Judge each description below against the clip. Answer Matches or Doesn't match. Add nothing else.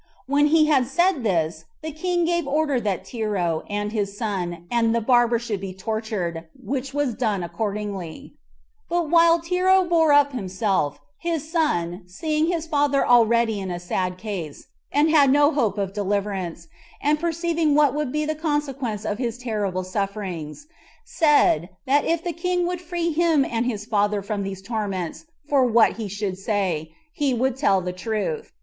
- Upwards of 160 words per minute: Matches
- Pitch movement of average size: Doesn't match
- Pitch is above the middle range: Matches